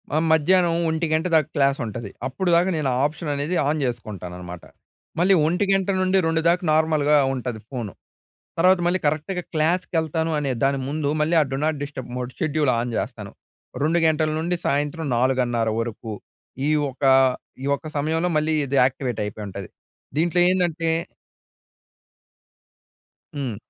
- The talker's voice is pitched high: No, medium, 150 Hz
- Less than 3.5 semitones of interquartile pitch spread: No, average, 4.4 semitones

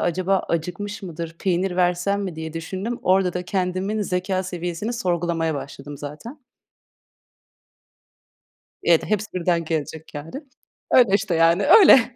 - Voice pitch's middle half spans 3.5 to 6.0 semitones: No, average, 3.1 semitones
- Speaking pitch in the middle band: Yes, medium, 180 Hz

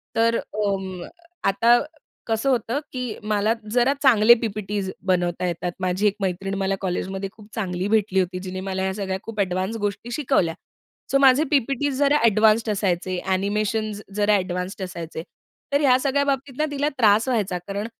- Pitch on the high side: Yes, high, 205 Hz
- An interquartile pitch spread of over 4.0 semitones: No, average, 3.7 semitones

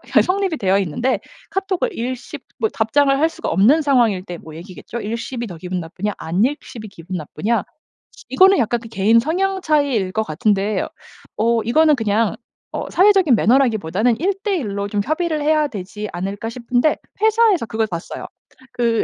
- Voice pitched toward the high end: Yes, high, 230 Hz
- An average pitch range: No, wide, 7.2 semitones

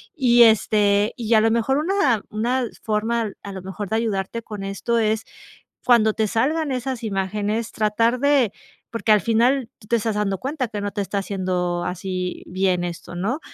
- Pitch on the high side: Yes, high, 220 Hz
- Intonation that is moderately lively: Yes, average, 3.1 semitones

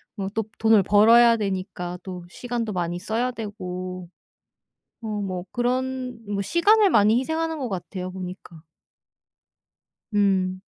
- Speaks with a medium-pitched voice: No, high, 205 Hz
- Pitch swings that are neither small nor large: Yes, average, 4.7 semitones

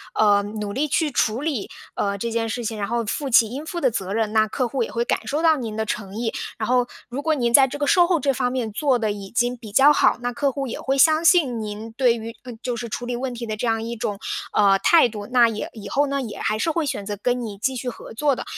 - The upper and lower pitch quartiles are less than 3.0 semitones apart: No, average, 3.8 semitones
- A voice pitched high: Yes, high, 235 Hz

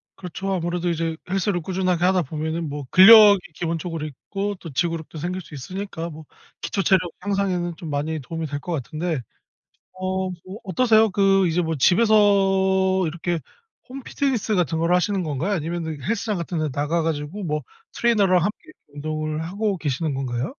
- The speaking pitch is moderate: Yes, medium, 175 Hz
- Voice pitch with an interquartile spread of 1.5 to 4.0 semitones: Yes, average, 3.6 semitones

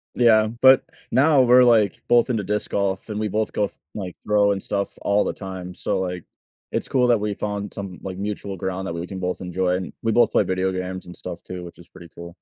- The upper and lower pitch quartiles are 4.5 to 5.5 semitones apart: No, average, 2.8 semitones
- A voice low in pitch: Yes, low, 100 Hz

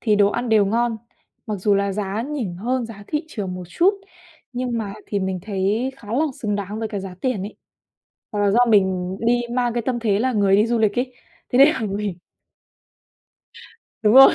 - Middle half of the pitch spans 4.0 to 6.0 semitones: No, average, 3.4 semitones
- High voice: Yes, high, 215 Hz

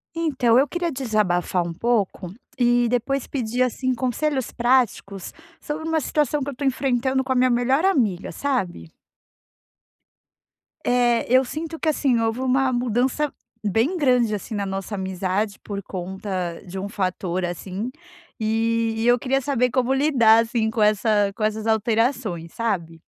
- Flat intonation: No, average, 4.3 semitones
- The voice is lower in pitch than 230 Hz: No, high, 235 Hz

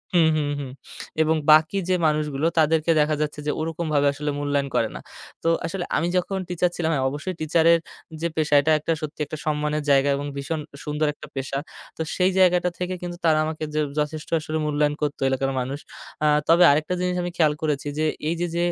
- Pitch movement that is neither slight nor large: No, narrow, 2.2 semitones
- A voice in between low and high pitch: Yes, medium, 155 Hz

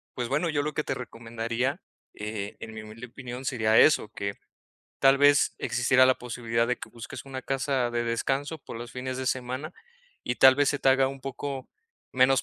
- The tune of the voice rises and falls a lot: No, narrow, 2.6 semitones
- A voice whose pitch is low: Yes, low, 130 Hz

